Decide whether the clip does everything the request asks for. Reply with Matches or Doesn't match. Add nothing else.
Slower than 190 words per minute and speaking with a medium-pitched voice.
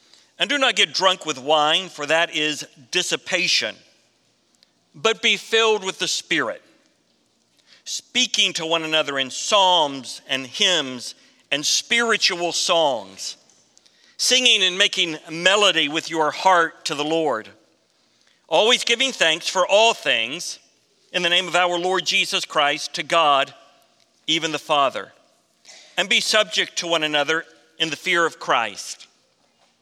Matches